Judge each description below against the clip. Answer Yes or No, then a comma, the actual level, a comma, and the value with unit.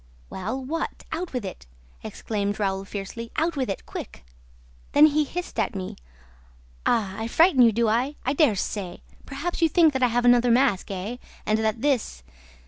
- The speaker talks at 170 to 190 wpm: Yes, average, 180 wpm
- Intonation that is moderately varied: No, wide, 5.8 semitones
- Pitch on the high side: Yes, high, 235 Hz